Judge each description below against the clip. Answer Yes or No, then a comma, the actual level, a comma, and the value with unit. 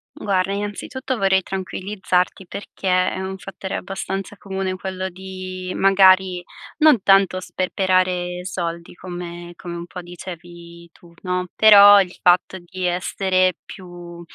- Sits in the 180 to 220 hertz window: Yes, medium, 185 Hz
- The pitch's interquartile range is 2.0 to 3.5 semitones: No, narrow, 1.5 semitones